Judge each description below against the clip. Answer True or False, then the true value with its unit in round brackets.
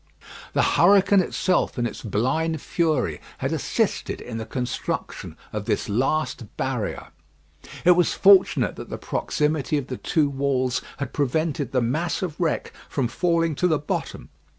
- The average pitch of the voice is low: False (150 Hz)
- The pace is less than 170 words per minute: True (150 wpm)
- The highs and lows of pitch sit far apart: False (4.7 semitones)